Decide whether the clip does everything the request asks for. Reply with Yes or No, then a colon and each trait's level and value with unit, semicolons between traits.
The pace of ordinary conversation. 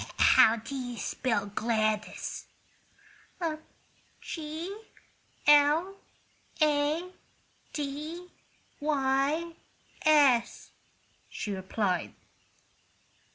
No: slow, 60 wpm